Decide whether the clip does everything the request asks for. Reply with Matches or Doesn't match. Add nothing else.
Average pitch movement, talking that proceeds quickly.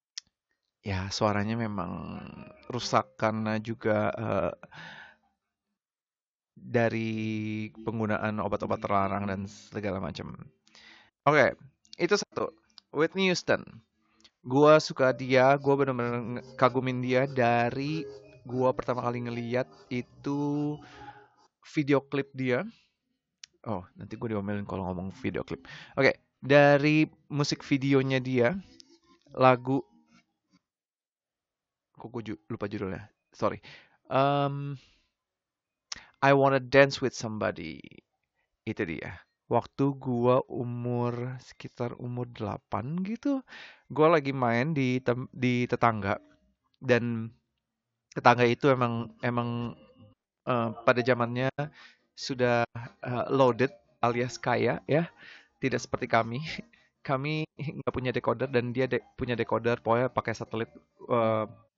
Doesn't match